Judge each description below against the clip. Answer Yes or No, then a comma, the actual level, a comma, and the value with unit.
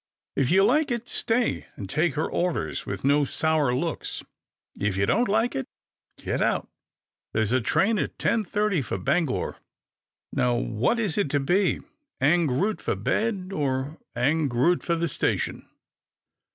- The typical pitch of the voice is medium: Yes, medium, 160 Hz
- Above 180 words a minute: No, average, 165 wpm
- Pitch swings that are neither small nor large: No, wide, 7.5 semitones